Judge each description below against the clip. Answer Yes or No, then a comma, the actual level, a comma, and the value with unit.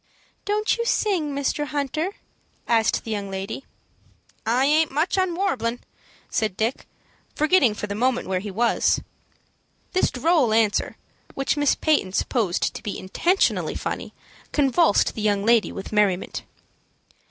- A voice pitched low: No, very high, 250 Hz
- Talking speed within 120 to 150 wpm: Yes, average, 140 wpm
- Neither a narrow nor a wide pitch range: No, wide, 6.7 semitones